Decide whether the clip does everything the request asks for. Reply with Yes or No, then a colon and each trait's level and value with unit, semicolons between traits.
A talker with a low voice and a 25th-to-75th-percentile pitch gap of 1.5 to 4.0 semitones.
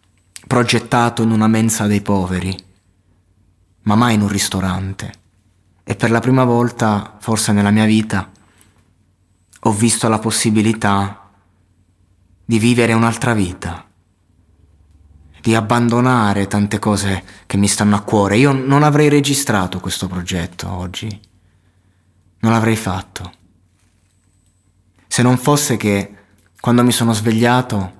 Yes: low, 100 Hz; average, 3.4 semitones